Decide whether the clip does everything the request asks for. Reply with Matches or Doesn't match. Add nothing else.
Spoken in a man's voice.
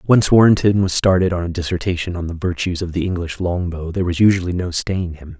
Matches